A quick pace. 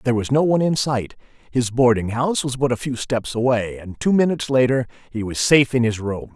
Yes: fast, 225 wpm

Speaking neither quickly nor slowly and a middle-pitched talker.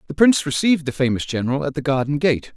No: fast, 235 wpm; medium, 150 Hz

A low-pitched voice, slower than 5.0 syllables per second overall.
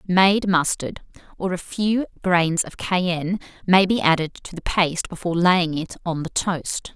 No: medium, 175 Hz; 4.4 syllables/s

